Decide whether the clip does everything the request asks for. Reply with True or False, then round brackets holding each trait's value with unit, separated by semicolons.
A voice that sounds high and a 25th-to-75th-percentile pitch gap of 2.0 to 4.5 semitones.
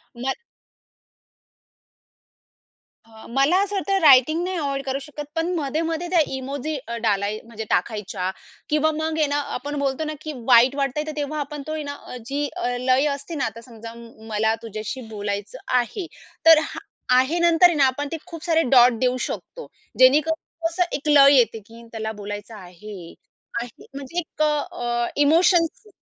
False (275 Hz; 5.2 semitones)